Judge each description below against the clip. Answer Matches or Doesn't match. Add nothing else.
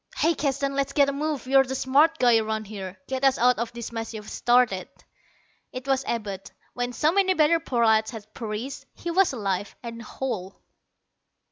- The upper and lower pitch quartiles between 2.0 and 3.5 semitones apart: Doesn't match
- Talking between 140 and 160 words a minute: Doesn't match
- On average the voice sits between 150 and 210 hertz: Doesn't match